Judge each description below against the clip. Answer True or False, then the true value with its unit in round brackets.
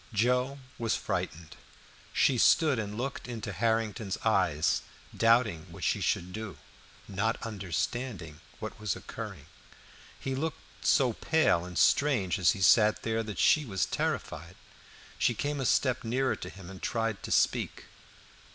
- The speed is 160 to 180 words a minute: False (145 wpm)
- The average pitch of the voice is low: True (110 Hz)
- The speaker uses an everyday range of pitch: True (4.7 semitones)